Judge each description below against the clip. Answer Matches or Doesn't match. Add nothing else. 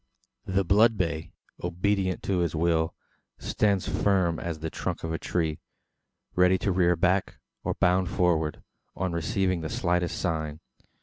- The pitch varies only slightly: Matches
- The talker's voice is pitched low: Matches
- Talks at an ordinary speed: Matches